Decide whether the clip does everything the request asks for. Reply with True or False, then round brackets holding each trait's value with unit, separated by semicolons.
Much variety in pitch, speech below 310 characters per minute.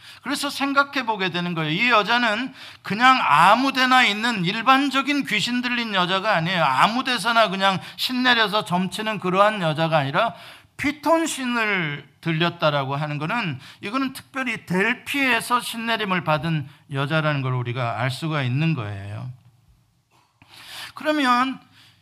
True (8.0 semitones; 300 characters per minute)